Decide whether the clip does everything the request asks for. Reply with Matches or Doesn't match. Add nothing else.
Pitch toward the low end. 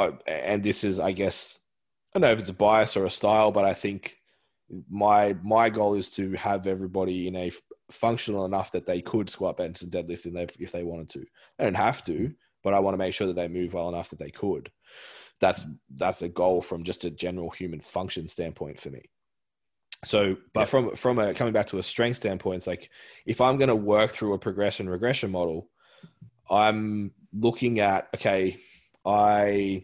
Matches